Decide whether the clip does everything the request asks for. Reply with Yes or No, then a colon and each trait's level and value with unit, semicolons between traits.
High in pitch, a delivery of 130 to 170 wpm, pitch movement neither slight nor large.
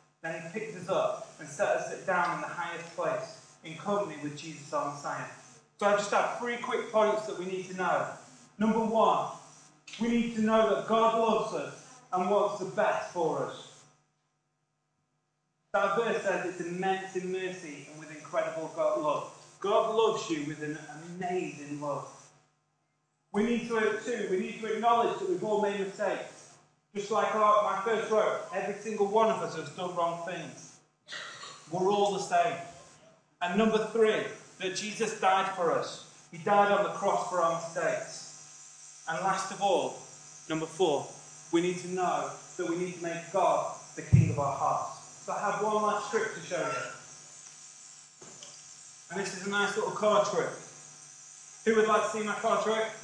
No: high, 195 Hz; average, 180 wpm; average, 4.6 semitones